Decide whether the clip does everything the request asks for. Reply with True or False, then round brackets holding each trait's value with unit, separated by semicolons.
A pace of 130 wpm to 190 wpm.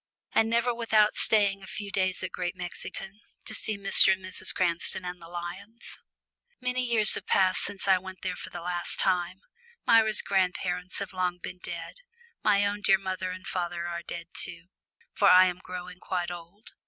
True (185 wpm)